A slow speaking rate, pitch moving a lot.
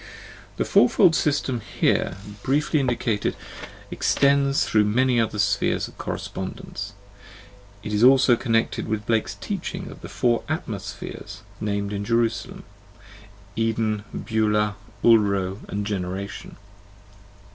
No: slow, 115 wpm; average, 2.9 semitones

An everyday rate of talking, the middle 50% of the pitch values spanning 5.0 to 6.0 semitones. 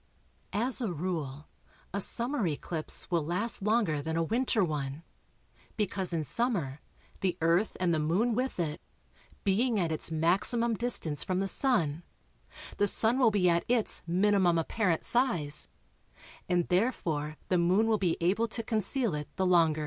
Yes: average, 155 wpm; wide, 5.4 semitones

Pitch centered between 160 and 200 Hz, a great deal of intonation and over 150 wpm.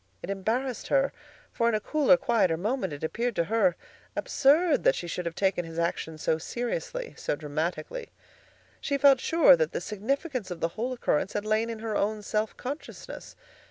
No: high, 220 Hz; wide, 7.3 semitones; average, 185 wpm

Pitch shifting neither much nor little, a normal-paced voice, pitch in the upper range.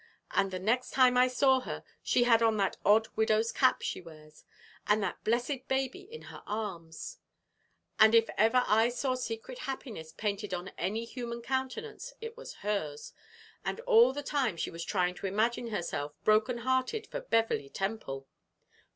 Yes: average, 4.6 semitones; average, 170 wpm; high, 225 Hz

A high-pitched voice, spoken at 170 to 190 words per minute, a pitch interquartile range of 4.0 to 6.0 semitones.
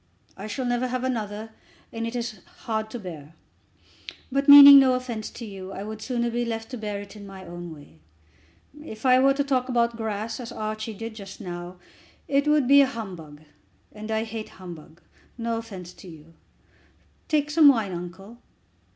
Yes: high, 220 Hz; average, 185 wpm; average, 4.4 semitones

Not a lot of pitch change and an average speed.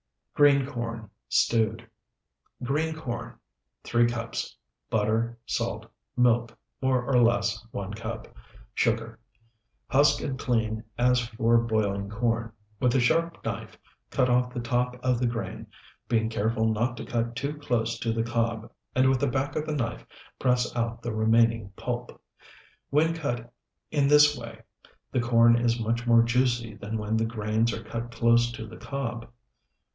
Yes: narrow, 1.7 semitones; average, 155 wpm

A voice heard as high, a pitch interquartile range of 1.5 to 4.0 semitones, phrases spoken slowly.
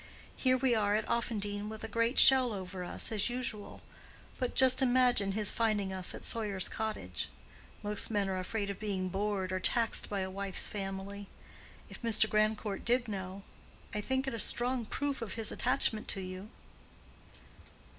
No: high, 210 Hz; average, 3.1 semitones; average, 170 wpm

